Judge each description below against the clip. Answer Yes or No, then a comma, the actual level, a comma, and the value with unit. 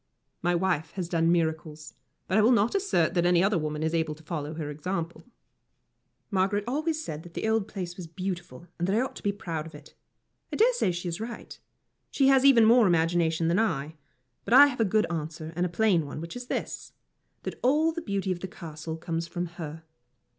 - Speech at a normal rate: No, fast, 220 wpm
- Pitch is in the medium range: Yes, medium, 175 Hz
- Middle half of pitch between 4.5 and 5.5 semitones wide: Yes, average, 5.1 semitones